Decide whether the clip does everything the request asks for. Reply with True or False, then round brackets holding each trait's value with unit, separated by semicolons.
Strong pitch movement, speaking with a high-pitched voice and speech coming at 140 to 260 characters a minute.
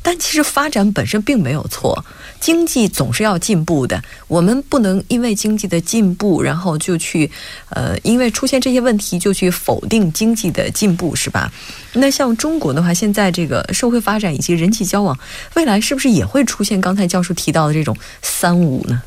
False (5.8 semitones; 200 Hz; 300 characters per minute)